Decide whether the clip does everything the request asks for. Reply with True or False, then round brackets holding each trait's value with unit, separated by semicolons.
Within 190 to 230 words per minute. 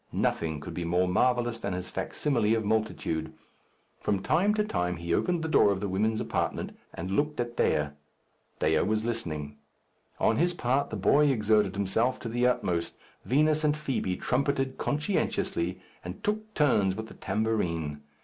False (165 wpm)